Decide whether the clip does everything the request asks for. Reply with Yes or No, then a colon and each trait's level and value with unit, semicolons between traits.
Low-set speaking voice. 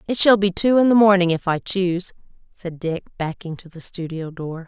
No: medium, 180 Hz